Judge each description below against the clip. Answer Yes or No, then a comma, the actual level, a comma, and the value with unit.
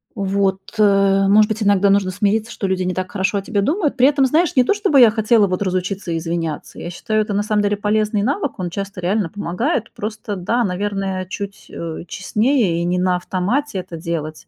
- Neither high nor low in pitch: No, high, 200 Hz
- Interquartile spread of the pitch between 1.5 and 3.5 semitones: Yes, average, 2.9 semitones